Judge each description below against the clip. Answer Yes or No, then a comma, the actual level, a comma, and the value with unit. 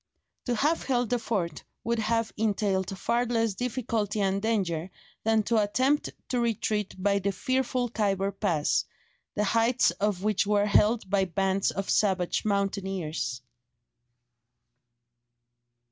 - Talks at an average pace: No, slow, 130 wpm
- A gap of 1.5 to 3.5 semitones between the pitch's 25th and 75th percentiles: Yes, average, 3.0 semitones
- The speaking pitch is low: No, high, 210 Hz